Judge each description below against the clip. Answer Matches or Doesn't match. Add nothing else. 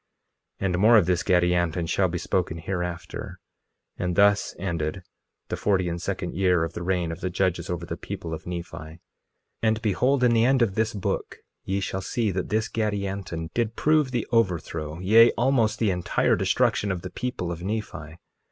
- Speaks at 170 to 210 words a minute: Matches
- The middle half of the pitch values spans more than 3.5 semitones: Matches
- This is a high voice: Doesn't match